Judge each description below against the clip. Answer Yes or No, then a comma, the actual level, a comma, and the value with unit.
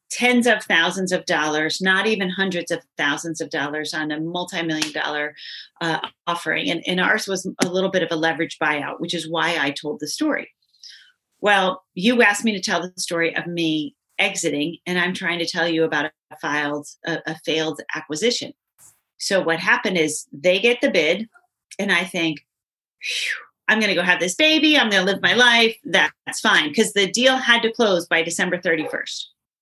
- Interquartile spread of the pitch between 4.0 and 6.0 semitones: Yes, average, 4.3 semitones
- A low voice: No, medium, 175 Hz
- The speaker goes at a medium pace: Yes, average, 190 wpm